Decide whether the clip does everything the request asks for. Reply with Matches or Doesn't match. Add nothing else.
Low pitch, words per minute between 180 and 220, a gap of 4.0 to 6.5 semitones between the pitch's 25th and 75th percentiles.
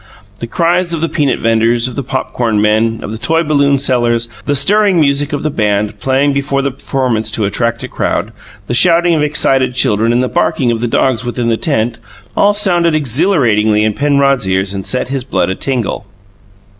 Matches